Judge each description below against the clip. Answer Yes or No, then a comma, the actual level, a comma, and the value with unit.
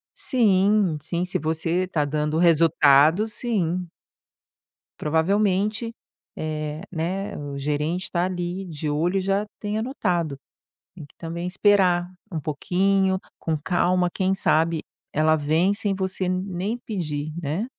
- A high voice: No, medium, 175 Hz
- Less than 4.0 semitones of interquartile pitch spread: Yes, average, 3.5 semitones